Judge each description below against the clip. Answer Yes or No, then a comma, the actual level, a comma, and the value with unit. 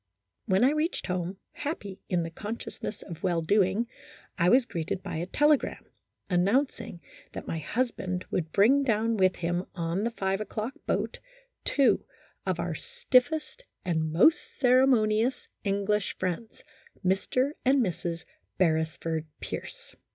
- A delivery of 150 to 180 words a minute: No, slow, 135 wpm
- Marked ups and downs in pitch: Yes, wide, 6.2 semitones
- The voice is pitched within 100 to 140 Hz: No, high, 200 Hz